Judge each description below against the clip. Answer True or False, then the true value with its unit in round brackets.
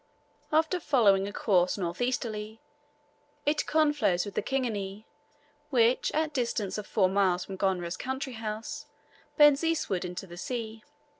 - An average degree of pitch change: False (6.0 semitones)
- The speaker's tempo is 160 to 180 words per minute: False (140 wpm)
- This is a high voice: True (220 Hz)